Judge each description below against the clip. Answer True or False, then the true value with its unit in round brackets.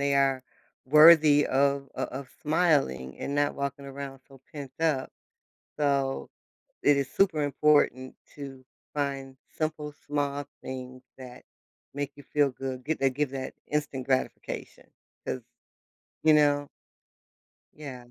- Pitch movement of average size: False (1.7 semitones)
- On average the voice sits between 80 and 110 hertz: False (140 Hz)